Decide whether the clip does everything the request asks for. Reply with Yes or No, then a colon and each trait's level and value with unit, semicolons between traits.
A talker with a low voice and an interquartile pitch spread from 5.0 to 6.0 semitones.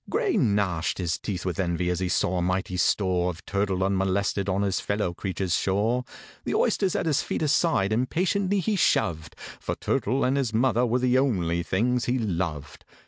Yes: low, 100 Hz; wide, 5.5 semitones